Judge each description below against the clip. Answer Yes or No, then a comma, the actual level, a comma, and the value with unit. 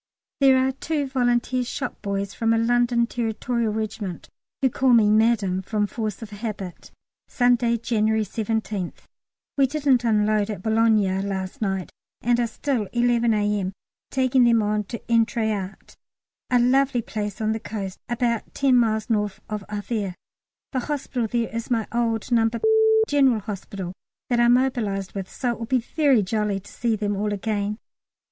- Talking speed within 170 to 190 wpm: No, average, 160 wpm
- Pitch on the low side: No, high, 225 Hz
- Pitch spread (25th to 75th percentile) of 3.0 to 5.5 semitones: No, narrow, 2.6 semitones